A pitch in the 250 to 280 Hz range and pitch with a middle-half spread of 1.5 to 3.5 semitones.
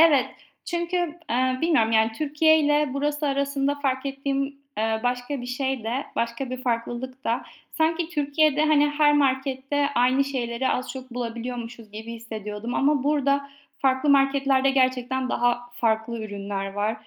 Yes: very high, 260 Hz; average, 3.1 semitones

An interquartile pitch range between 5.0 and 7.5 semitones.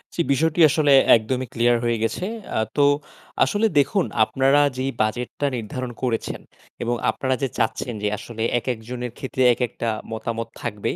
No: average, 2.9 semitones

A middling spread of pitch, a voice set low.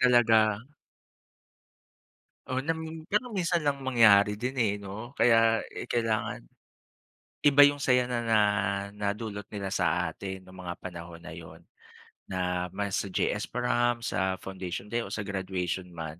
Yes: average, 4.7 semitones; low, 105 Hz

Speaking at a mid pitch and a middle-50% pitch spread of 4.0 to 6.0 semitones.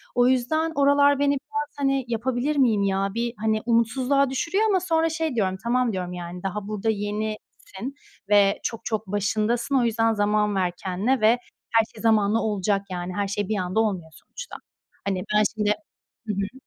No: high, 220 Hz; average, 4.5 semitones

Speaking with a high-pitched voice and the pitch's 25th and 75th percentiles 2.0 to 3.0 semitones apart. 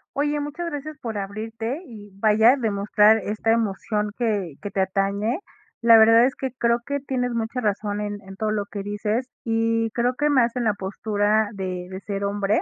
Yes: high, 220 Hz; average, 2.7 semitones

